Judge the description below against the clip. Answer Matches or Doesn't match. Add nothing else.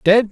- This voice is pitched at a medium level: Doesn't match